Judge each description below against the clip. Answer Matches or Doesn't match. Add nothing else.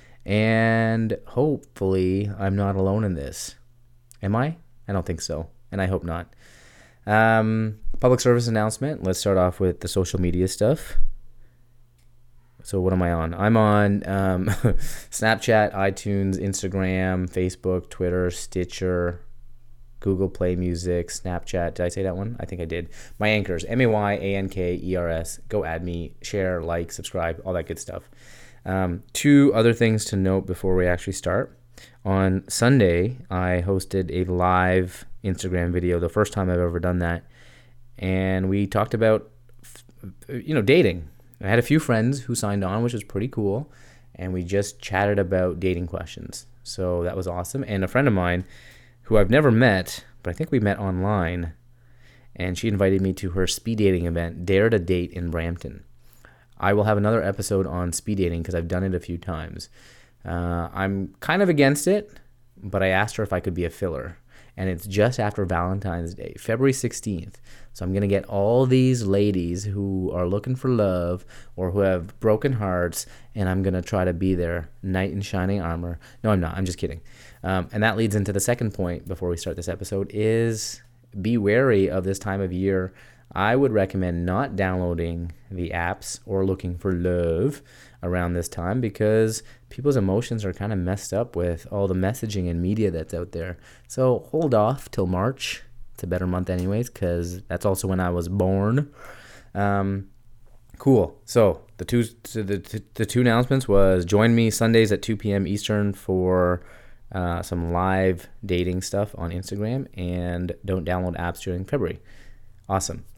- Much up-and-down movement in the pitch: Doesn't match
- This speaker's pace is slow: Doesn't match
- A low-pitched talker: Matches